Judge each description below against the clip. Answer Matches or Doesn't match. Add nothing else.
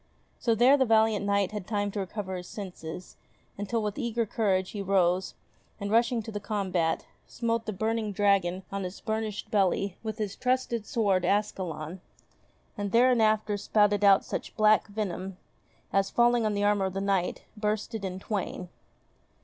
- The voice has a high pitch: Matches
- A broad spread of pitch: Doesn't match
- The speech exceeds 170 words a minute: Doesn't match